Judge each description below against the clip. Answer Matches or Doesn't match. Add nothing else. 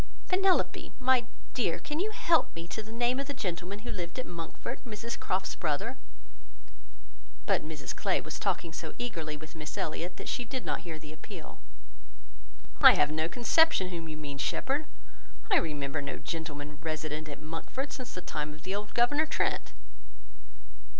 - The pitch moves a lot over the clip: Matches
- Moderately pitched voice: Matches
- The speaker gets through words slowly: Doesn't match